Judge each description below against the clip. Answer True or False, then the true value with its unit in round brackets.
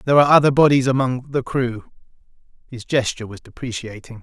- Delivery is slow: False (155 wpm)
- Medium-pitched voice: False (125 Hz)